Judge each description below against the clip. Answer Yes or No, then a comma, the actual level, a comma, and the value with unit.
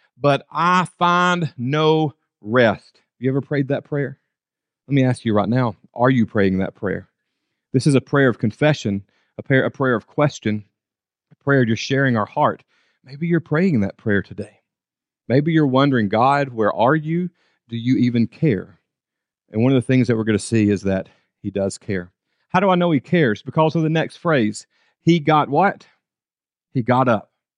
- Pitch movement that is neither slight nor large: No, wide, 6.0 semitones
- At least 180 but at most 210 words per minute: Yes, average, 195 wpm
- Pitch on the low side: Yes, low, 130 Hz